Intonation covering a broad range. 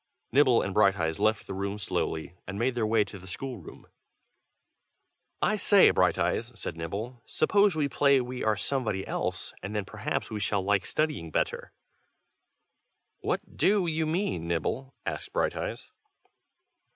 Yes: wide, 5.8 semitones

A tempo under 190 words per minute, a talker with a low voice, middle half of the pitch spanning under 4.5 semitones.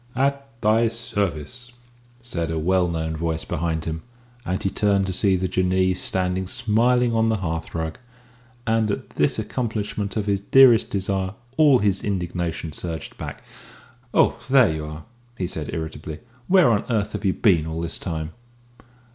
No: average, 160 wpm; very low, 95 Hz; wide, 5.4 semitones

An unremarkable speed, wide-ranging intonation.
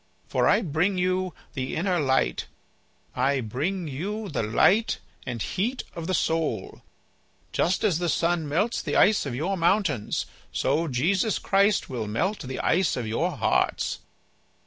Yes: average, 150 wpm; wide, 6.4 semitones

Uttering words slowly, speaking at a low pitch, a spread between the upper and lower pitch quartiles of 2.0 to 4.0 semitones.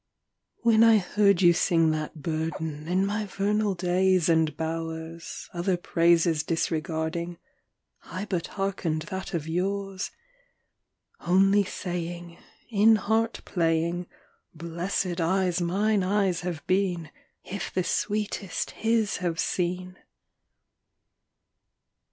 No: slow, 110 wpm; medium, 180 Hz; average, 2.9 semitones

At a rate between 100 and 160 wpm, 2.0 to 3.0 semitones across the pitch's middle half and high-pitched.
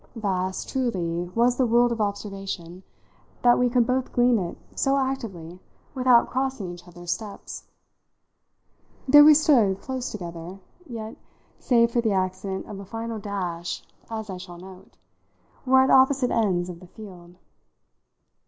No: average, 150 wpm; average, 5.1 semitones; high, 215 Hz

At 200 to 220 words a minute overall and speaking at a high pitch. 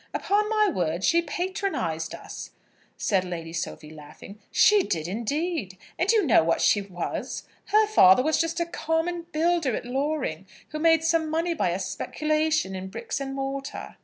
No: average, 165 wpm; very high, 285 Hz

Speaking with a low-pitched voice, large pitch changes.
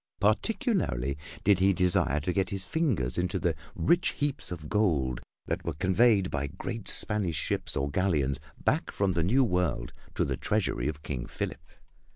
Yes: very low, 90 Hz; wide, 6.4 semitones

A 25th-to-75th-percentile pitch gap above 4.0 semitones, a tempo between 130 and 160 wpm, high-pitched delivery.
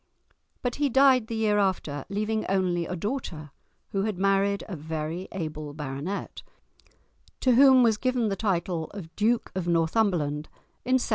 Yes: wide, 5.4 semitones; average, 155 wpm; high, 195 Hz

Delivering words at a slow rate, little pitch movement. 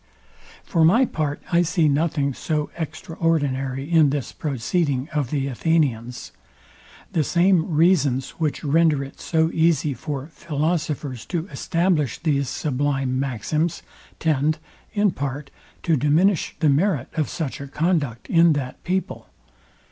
No: slow, 130 wpm; average, 3.2 semitones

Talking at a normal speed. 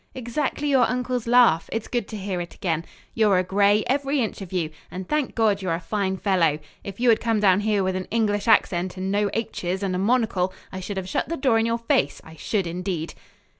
No: fast, 230 wpm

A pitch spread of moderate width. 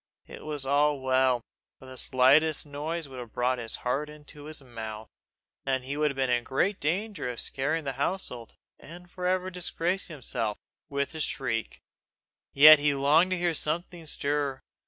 Yes: average, 3.6 semitones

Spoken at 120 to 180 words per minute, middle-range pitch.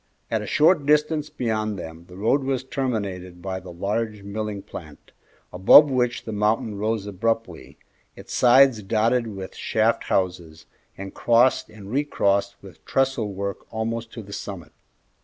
No: average, 150 wpm; low, 110 Hz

